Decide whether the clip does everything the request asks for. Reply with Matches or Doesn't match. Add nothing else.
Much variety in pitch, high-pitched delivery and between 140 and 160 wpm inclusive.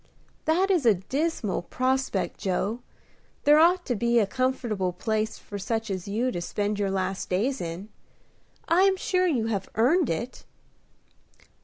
Matches